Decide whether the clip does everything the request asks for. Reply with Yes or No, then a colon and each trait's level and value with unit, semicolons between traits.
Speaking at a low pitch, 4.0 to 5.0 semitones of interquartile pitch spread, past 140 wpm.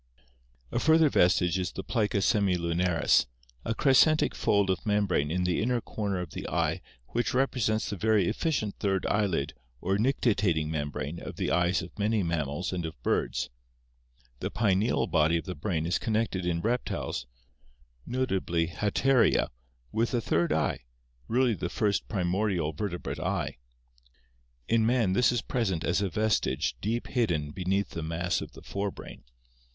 Yes: very low, 95 Hz; average, 4.5 semitones; average, 155 wpm